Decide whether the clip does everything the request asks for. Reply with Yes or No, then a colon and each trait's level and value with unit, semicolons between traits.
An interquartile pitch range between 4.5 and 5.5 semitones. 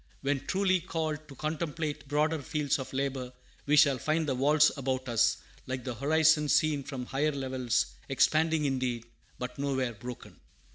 No: average, 2.9 semitones